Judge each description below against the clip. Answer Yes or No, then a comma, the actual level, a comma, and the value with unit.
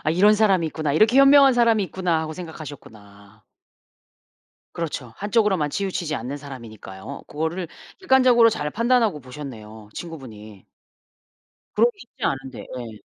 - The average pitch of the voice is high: No, medium, 160 Hz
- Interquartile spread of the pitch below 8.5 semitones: No, wide, 8.8 semitones